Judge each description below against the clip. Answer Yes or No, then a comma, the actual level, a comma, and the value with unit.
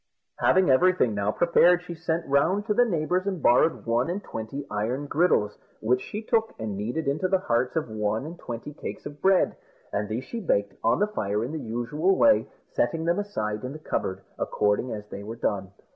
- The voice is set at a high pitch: No, medium, 140 Hz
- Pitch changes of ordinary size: No, wide, 8.5 semitones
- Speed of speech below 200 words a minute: No, fast, 205 wpm